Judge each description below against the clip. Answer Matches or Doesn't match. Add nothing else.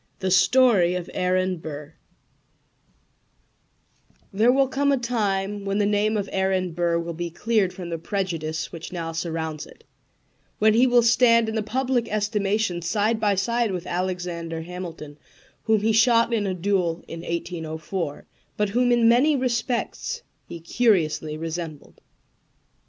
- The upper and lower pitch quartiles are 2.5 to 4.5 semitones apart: Doesn't match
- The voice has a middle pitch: Doesn't match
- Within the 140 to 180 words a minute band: Matches